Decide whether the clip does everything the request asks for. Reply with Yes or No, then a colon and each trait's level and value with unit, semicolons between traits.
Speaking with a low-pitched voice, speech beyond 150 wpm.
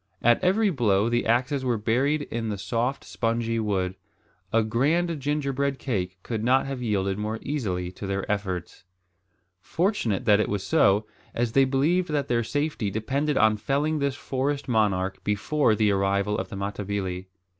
Yes: low, 115 Hz; average, 165 wpm